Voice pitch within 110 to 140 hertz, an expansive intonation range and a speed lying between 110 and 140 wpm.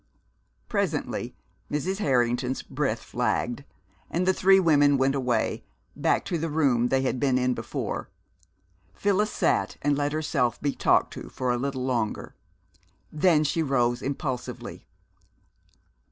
No: low, 135 Hz; average, 3.7 semitones; slow, 135 wpm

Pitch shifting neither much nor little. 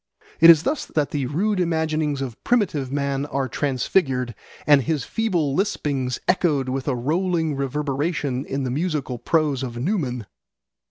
Yes: average, 3.7 semitones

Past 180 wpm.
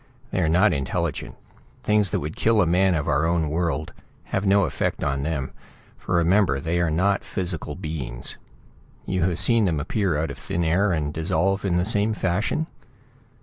Yes: average, 190 wpm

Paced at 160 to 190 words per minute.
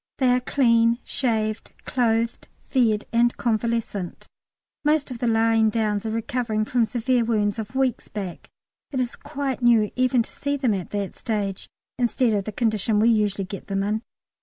Yes: average, 170 wpm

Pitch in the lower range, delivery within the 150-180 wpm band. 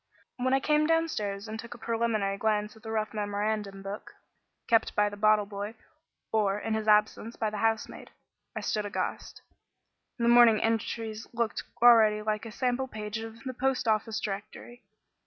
No: high, 220 Hz; average, 170 wpm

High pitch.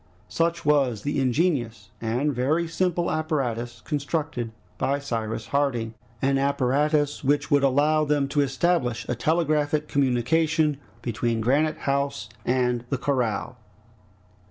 No: medium, 140 Hz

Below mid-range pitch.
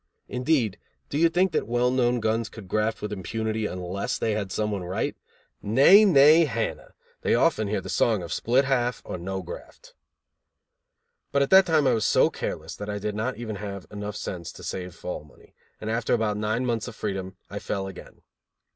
Yes: low, 110 Hz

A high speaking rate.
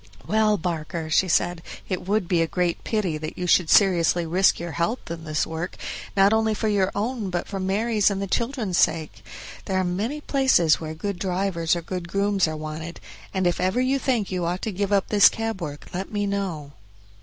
Yes: fast, 210 wpm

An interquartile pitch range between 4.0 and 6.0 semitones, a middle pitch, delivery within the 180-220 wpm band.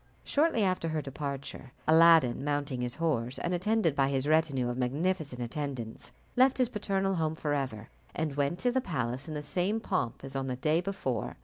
Yes: average, 5.2 semitones; medium, 150 Hz; average, 185 wpm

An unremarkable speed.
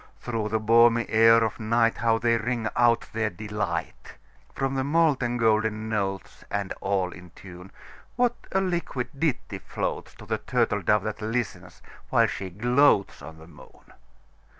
No: slow, 130 wpm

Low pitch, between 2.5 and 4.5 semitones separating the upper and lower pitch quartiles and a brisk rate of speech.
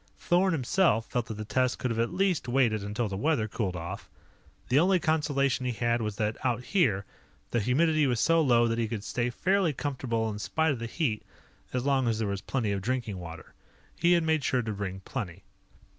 No: low, 120 Hz; average, 5.3 semitones; fast, 215 wpm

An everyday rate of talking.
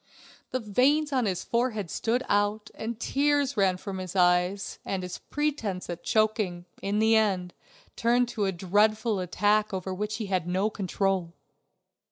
Yes: average, 160 wpm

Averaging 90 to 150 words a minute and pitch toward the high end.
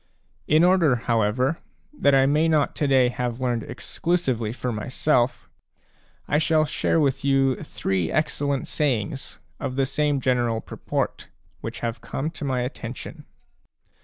No: average, 140 wpm; low, 135 Hz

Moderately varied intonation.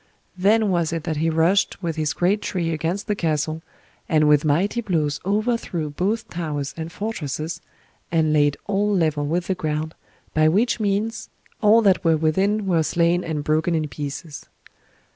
Yes: average, 4.2 semitones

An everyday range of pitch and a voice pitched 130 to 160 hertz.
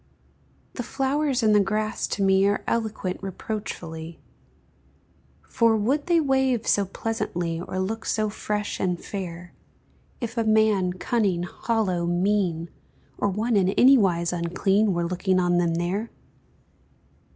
No: average, 4.0 semitones; high, 200 Hz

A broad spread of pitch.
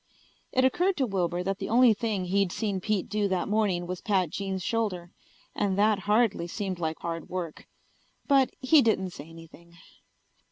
No: average, 3.6 semitones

